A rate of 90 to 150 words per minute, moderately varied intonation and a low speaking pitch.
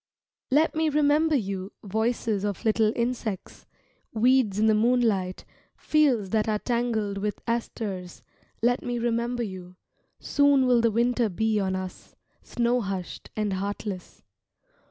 No: slow, 135 wpm; average, 3.4 semitones; high, 225 Hz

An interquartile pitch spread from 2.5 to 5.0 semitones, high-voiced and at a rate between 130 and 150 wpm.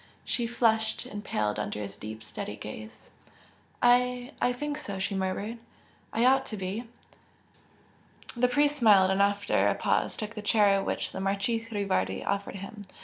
No: average, 3.8 semitones; high, 205 Hz; average, 160 wpm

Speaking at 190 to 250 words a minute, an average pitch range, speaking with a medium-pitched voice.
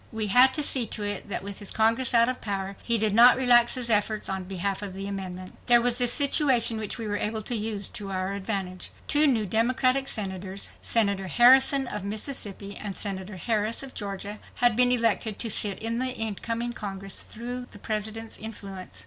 No: average, 200 wpm; average, 3.3 semitones; high, 220 Hz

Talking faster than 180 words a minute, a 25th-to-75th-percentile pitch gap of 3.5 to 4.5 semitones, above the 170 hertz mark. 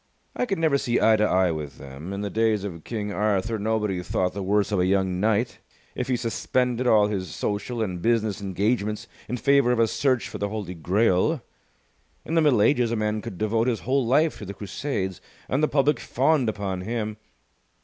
No: fast, 205 wpm; average, 3.9 semitones; low, 110 Hz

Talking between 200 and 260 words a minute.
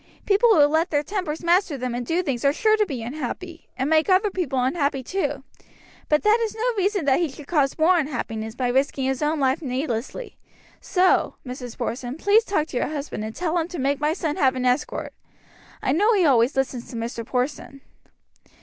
Yes: fast, 205 wpm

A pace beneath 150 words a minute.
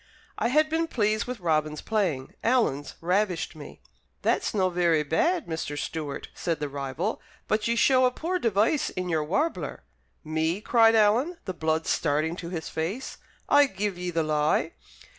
No: average, 165 wpm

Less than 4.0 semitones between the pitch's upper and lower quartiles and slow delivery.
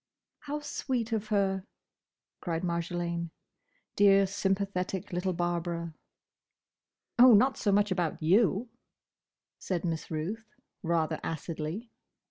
Yes: average, 3.4 semitones; slow, 100 wpm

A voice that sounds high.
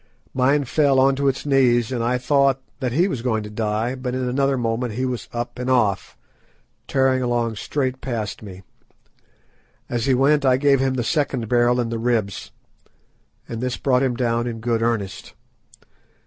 No: low, 125 Hz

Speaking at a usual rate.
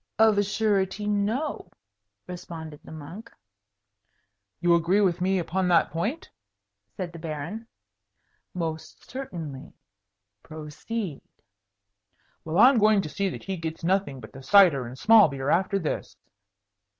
No: slow, 130 wpm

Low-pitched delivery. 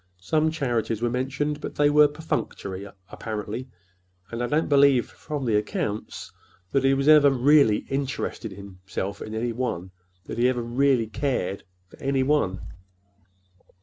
Yes: low, 125 Hz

